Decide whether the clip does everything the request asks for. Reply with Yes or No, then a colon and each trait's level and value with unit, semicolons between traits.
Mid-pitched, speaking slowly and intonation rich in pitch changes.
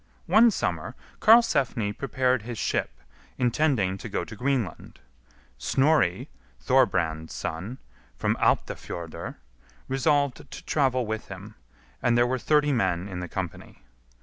No: low, 120 Hz; slow, 120 wpm; wide, 6.5 semitones